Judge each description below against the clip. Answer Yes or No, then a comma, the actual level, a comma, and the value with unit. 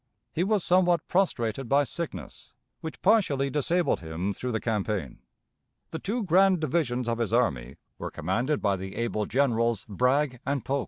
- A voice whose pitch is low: Yes, low, 125 Hz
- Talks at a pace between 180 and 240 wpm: No, average, 160 wpm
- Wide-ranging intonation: Yes, wide, 7.1 semitones